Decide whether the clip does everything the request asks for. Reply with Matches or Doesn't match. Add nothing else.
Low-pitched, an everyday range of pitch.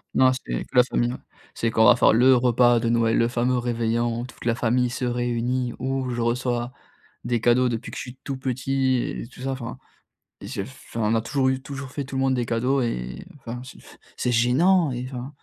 Doesn't match